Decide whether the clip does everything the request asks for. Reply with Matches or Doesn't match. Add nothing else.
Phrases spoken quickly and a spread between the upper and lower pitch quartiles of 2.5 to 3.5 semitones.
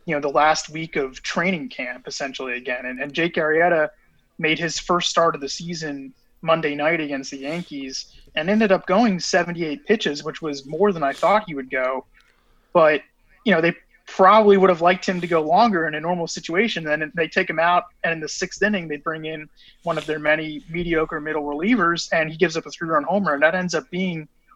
Matches